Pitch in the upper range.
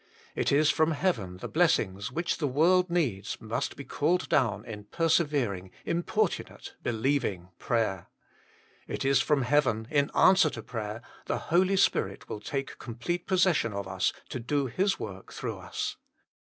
No: low, 135 Hz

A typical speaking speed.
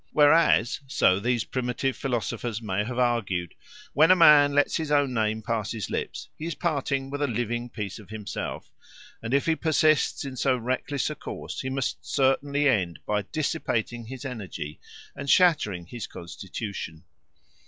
Yes: average, 165 wpm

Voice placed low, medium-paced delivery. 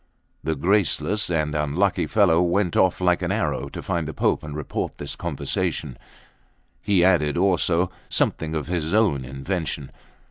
Yes: very low, 85 Hz; average, 150 wpm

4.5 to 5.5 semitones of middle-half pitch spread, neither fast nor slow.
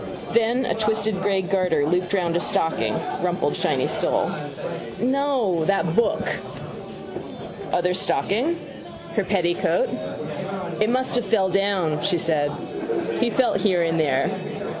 No: average, 4.8 semitones; slow, 125 wpm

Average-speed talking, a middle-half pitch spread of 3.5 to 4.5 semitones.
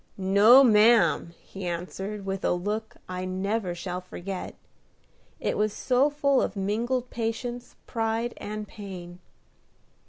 No: slow, 125 wpm; average, 3.8 semitones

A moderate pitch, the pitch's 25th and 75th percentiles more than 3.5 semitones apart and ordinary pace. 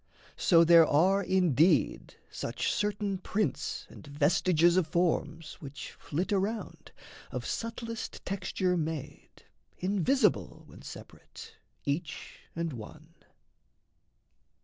No: medium, 175 Hz; average, 4.0 semitones; slow, 100 wpm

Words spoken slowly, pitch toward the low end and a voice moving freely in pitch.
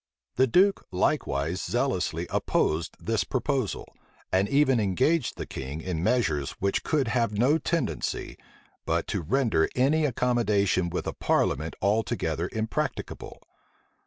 Yes: slow, 125 wpm; low, 110 Hz; wide, 6.5 semitones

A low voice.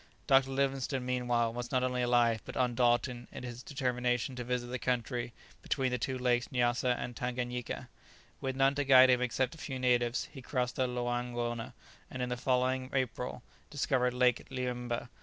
Yes: low, 125 Hz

